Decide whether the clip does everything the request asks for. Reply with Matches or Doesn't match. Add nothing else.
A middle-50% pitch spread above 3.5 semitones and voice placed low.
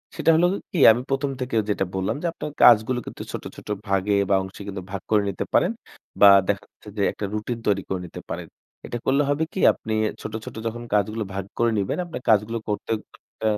Matches